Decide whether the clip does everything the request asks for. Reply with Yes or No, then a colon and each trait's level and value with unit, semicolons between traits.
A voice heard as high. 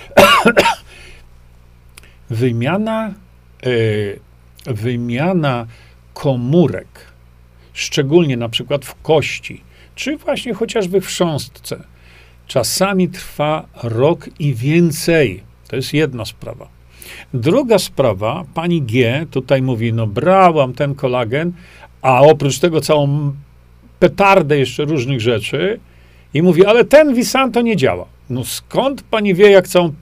No: low, 135 Hz